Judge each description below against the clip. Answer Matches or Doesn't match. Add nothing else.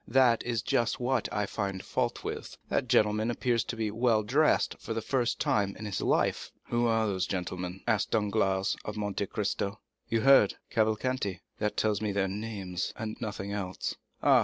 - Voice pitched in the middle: Doesn't match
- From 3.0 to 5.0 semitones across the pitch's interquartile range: Doesn't match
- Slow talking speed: Doesn't match